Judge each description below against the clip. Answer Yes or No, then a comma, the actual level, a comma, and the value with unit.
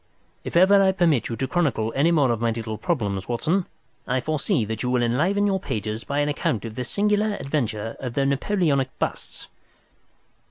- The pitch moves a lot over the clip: Yes, wide, 7.1 semitones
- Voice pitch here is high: No, low, 135 Hz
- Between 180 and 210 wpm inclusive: Yes, average, 190 wpm